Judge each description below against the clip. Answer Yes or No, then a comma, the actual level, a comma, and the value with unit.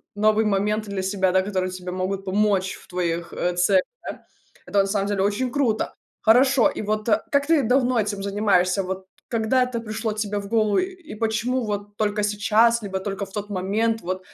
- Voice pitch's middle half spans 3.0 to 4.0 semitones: No, narrow, 2.5 semitones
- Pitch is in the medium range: No, high, 205 Hz